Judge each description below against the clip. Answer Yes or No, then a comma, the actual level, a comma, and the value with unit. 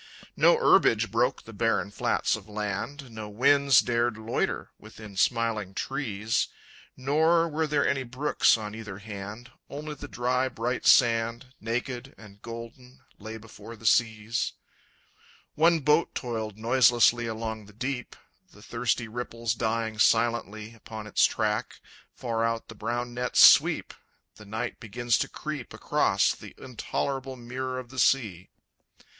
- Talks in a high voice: No, low, 115 Hz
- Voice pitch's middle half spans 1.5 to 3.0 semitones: Yes, average, 2.7 semitones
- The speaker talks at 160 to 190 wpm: No, average, 140 wpm